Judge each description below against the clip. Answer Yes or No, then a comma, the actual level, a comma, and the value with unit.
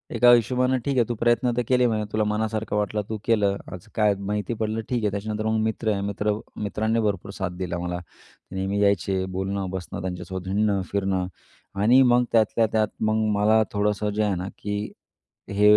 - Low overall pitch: Yes, low, 105 Hz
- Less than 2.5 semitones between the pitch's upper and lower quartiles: Yes, narrow, 2.1 semitones